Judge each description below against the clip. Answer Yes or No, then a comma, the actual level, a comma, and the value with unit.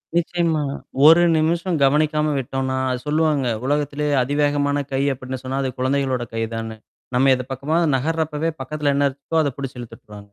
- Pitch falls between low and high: Yes, medium, 145 Hz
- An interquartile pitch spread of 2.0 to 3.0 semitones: Yes, average, 2.7 semitones